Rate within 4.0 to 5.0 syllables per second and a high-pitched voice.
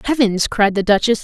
No: 5.4 syllables/s; high, 215 Hz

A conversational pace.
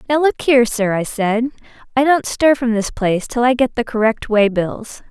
No: fast, 225 wpm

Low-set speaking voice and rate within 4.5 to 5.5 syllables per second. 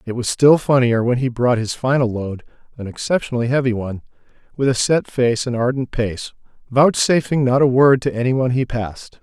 Yes: low, 125 Hz; 4.6 syllables/s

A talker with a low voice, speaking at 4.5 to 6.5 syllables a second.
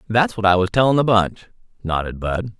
Yes: low, 105 Hz; 5.4 syllables/s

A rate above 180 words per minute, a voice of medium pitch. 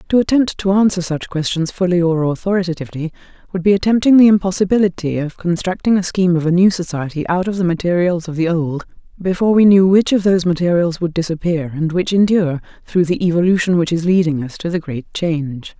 Yes: average, 200 wpm; medium, 175 Hz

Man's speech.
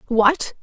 No: female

